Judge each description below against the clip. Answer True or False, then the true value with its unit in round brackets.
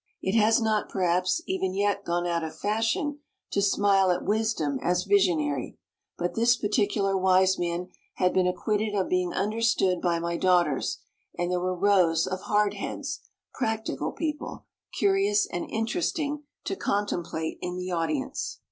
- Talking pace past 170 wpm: False (145 wpm)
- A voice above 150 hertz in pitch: True (190 Hz)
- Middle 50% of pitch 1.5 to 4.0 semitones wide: True (3.1 semitones)